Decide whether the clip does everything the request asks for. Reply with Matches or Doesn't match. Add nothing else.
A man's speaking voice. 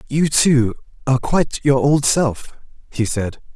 Matches